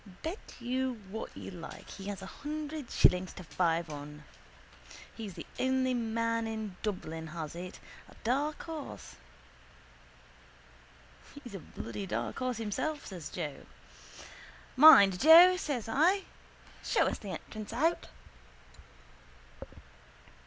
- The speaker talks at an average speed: No, slow, 120 wpm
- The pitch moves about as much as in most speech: No, wide, 7.6 semitones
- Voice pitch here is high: Yes, high, 225 Hz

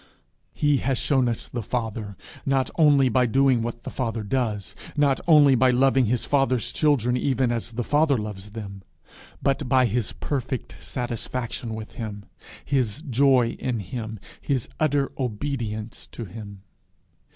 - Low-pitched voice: Yes, low, 125 Hz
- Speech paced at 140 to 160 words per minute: Yes, average, 150 wpm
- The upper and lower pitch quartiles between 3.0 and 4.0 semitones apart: Yes, average, 3.4 semitones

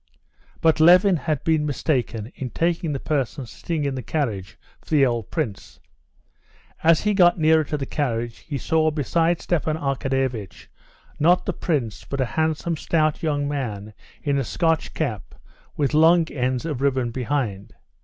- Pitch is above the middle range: No, medium, 145 Hz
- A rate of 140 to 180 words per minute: Yes, average, 160 wpm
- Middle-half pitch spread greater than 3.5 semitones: Yes, average, 4.0 semitones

